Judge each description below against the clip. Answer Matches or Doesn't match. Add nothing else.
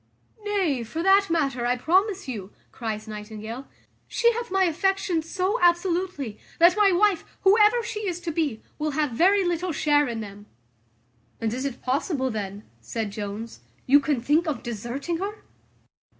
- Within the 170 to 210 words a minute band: Doesn't match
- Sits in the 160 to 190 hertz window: Doesn't match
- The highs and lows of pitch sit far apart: Matches